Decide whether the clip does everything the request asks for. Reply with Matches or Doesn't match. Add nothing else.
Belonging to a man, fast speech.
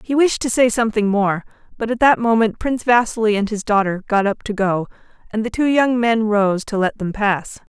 Doesn't match